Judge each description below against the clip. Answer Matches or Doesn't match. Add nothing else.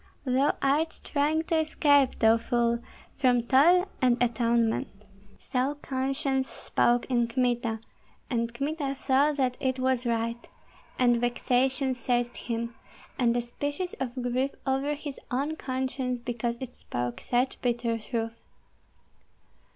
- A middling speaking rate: Doesn't match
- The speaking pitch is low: Doesn't match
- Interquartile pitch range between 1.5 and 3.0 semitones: Matches